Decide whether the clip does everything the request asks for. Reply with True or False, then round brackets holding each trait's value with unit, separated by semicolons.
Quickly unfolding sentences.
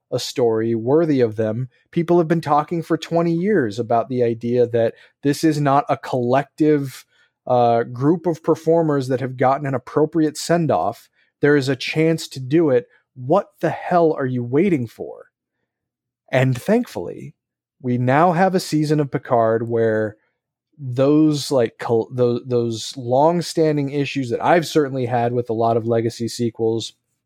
False (160 wpm)